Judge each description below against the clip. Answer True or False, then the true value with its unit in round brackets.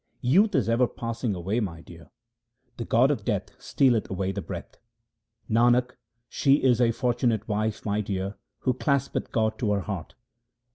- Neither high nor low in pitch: False (115 Hz)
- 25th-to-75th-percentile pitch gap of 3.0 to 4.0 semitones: True (3.4 semitones)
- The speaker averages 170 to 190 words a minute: False (160 wpm)